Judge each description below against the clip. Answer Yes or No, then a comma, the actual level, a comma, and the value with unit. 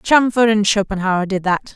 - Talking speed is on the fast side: No, average, 170 wpm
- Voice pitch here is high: Yes, high, 205 Hz